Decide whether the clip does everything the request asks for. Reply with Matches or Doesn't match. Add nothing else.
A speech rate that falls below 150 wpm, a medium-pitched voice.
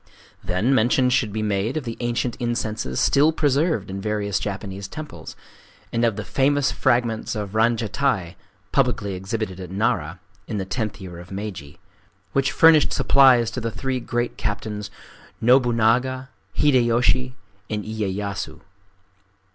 Doesn't match